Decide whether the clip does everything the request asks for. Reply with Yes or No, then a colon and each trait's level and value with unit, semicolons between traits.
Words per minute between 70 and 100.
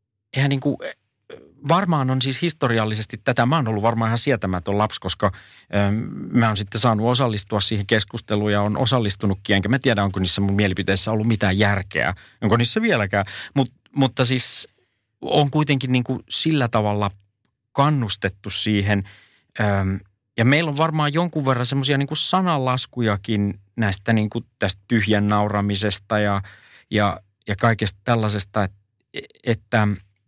No: average, 145 wpm